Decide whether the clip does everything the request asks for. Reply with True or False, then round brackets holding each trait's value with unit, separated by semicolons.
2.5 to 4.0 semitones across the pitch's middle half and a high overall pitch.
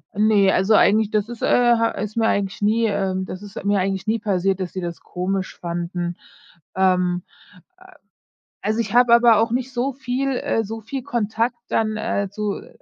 True (3.1 semitones; 210 Hz)